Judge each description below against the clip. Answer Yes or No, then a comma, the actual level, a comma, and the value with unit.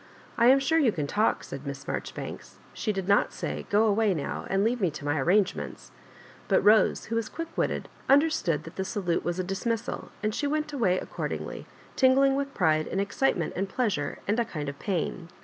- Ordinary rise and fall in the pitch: No, wide, 5.8 semitones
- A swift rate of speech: Yes, fast, 220 wpm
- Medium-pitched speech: No, high, 205 Hz